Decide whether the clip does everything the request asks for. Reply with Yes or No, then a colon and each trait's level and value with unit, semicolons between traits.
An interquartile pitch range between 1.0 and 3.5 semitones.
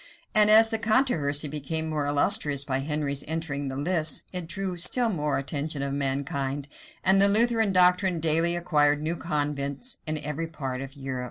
No: average, 4.3 semitones